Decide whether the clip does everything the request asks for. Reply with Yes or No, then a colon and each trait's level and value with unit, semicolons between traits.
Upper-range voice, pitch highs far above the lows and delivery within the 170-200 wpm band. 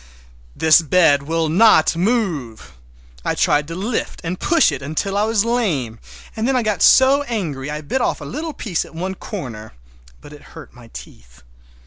No: medium, 165 Hz; wide, 7.8 semitones; average, 175 wpm